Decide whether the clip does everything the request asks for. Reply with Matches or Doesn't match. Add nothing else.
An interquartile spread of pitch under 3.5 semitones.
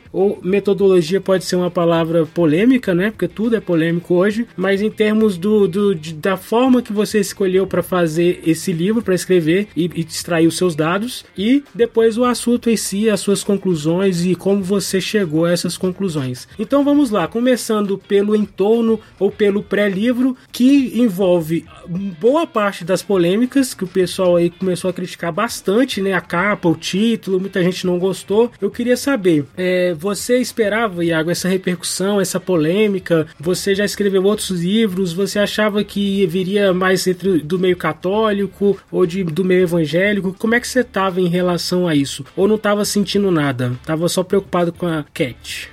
Matches